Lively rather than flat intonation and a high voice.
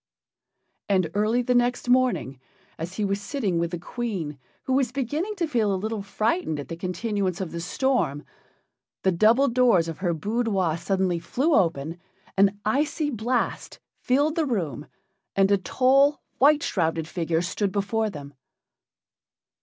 Yes: wide, 6.6 semitones; high, 205 Hz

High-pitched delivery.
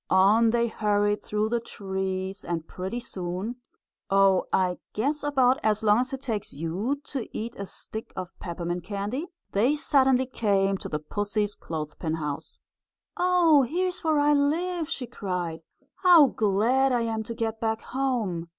Yes: high, 220 Hz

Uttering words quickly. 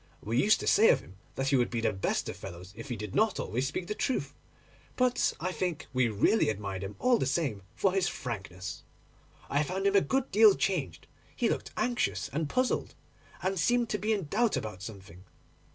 Yes: fast, 210 wpm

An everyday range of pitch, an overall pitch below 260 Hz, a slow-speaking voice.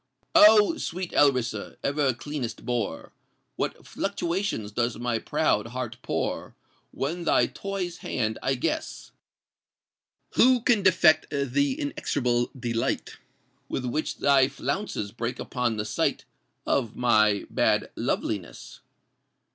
No: wide, 6.2 semitones; low, 135 Hz; slow, 110 wpm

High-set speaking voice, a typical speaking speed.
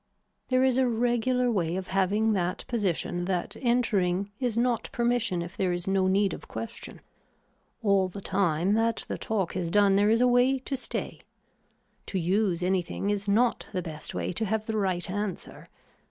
Yes: high, 200 Hz; average, 180 wpm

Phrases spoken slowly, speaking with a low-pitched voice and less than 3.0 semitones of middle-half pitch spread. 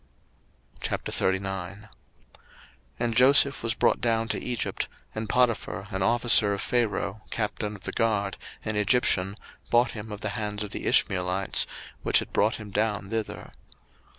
No: average, 145 wpm; low, 105 Hz; narrow, 2.4 semitones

